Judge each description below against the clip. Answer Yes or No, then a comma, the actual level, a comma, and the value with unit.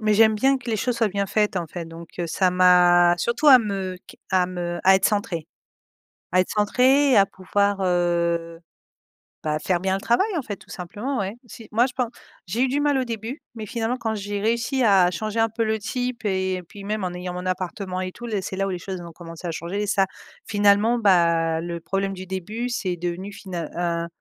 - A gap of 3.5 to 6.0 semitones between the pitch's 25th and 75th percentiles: Yes, average, 4.0 semitones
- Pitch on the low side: No, high, 195 Hz